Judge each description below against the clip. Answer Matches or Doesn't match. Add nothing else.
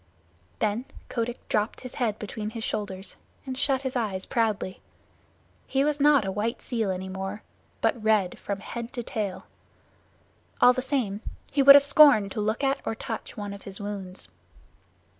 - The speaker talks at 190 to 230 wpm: Doesn't match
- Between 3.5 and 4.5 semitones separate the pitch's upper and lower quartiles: Matches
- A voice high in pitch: Matches